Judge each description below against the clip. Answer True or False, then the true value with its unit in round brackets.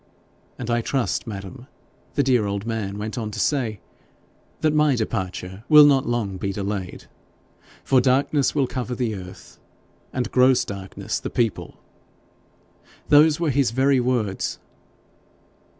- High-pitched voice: False (120 Hz)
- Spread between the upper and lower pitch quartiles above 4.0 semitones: True (4.7 semitones)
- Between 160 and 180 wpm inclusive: False (135 wpm)